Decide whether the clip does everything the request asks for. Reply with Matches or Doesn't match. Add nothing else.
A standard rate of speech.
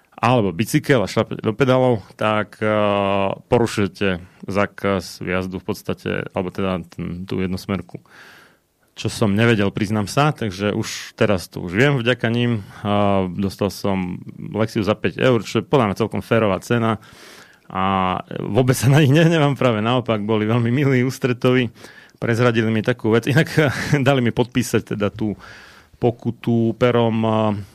Matches